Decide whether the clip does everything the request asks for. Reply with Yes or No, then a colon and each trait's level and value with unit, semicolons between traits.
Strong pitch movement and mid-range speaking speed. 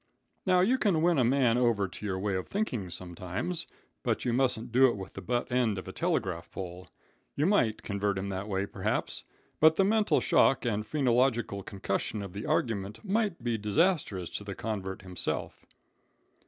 Yes: wide, 5.8 semitones; average, 180 wpm